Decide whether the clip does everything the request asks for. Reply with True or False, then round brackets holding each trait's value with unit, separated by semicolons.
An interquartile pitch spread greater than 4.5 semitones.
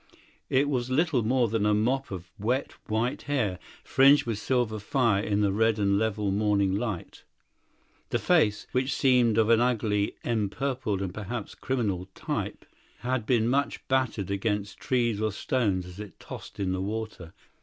False (3.8 semitones)